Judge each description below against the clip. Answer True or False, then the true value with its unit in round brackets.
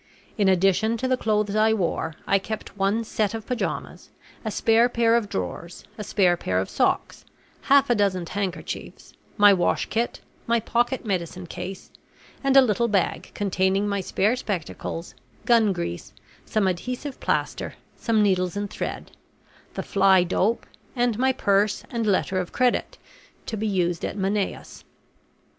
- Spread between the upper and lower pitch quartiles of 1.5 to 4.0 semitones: True (3.4 semitones)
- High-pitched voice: True (205 Hz)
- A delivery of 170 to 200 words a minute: False (155 wpm)